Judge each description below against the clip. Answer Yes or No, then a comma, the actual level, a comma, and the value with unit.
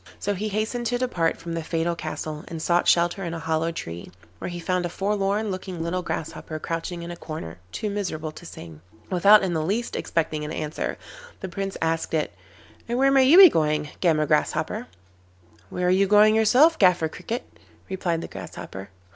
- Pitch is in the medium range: Yes, medium, 175 Hz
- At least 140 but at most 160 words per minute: No, average, 190 wpm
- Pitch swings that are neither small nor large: Yes, average, 4.1 semitones